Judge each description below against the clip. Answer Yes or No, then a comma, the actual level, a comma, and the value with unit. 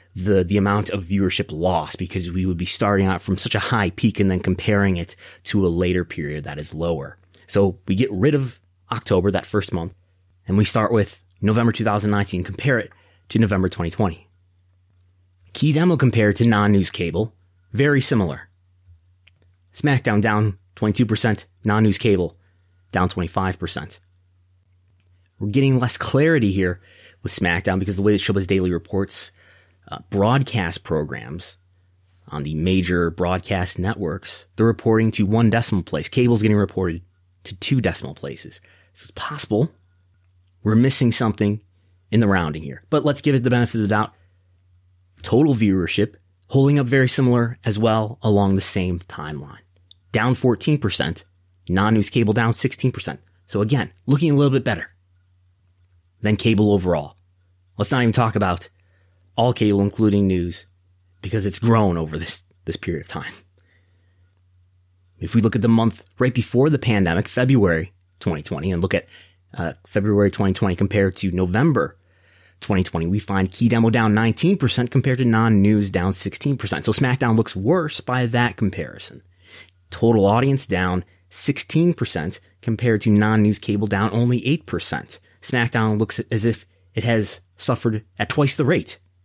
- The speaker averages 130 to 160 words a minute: Yes, average, 155 wpm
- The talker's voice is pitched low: Yes, low, 100 Hz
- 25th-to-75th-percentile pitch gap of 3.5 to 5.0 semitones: Yes, average, 3.8 semitones